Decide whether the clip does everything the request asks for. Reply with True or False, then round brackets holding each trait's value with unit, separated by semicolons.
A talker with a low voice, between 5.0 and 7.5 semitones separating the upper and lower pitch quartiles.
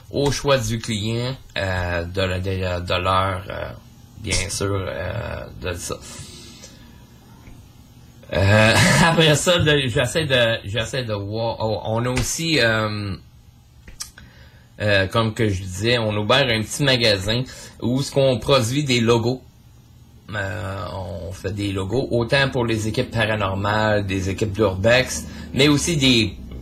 False (110 Hz; 4.3 semitones)